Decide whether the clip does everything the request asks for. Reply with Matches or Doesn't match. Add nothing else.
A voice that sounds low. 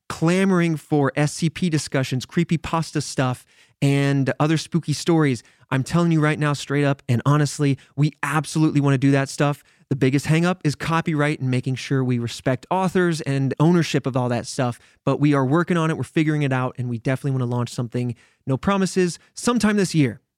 Doesn't match